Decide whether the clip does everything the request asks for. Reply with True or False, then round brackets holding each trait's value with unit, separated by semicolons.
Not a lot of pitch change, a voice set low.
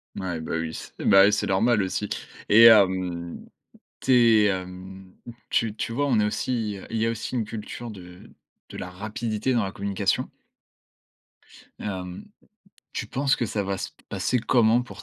False (3.4 semitones; 105 Hz)